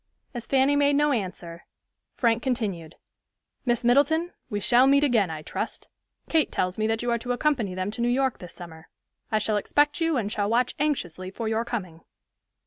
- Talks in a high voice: Yes, high, 235 Hz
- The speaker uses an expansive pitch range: Yes, wide, 5.7 semitones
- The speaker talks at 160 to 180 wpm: No, average, 190 wpm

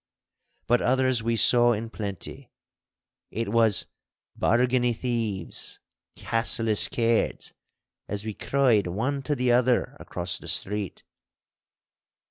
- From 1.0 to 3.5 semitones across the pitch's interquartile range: Yes, average, 2.8 semitones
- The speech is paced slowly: Yes, slow, 105 wpm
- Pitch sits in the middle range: No, low, 115 Hz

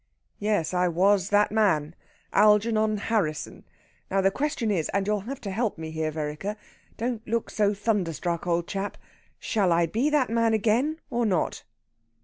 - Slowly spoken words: No, average, 160 wpm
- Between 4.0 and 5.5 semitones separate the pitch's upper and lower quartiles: Yes, average, 4.3 semitones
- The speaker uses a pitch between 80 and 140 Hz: No, high, 205 Hz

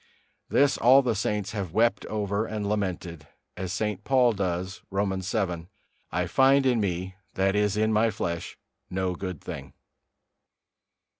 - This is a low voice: Yes, low, 100 Hz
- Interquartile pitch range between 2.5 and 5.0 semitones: Yes, average, 2.9 semitones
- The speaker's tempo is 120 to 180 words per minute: Yes, average, 145 wpm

